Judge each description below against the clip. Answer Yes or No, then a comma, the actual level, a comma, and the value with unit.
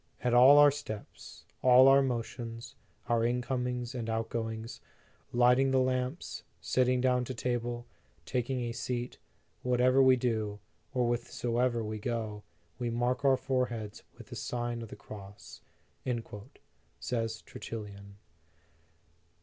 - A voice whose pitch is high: No, low, 120 Hz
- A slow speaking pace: Yes, slow, 125 wpm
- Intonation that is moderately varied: No, narrow, 1.8 semitones